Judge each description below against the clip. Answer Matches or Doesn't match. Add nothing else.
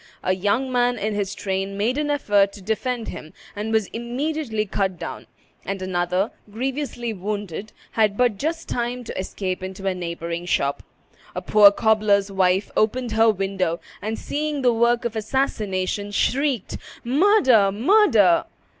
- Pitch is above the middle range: Matches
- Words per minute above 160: Doesn't match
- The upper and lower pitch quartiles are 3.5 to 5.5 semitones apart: Matches